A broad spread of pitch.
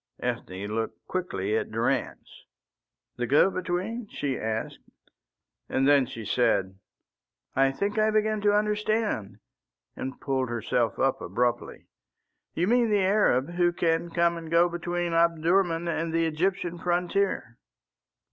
Yes: wide, 6.7 semitones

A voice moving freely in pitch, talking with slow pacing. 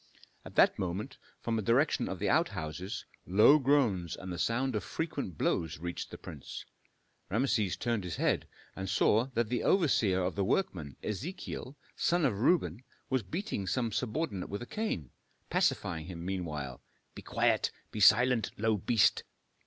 No: wide, 6.0 semitones; average, 160 wpm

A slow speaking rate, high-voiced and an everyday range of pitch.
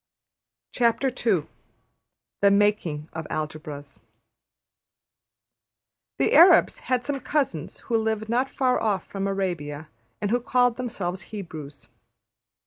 No: slow, 100 wpm; high, 200 Hz; wide, 7.7 semitones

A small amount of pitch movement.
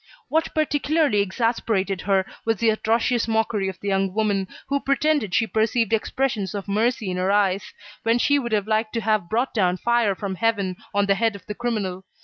No: average, 3.1 semitones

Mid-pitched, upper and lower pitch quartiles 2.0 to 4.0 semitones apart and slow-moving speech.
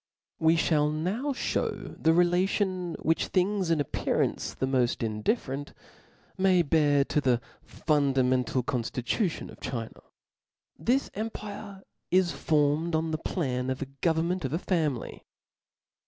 No: medium, 160 Hz; average, 5.2 semitones; slow, 125 wpm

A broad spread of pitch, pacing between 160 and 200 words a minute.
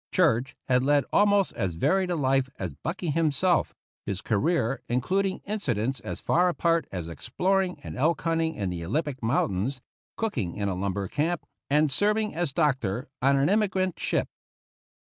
Yes: wide, 7.5 semitones; average, 180 wpm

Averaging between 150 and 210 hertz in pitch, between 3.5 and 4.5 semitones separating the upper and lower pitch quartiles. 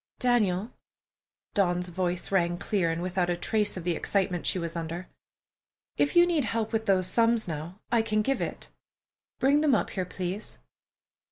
Yes: high, 190 Hz; average, 4.0 semitones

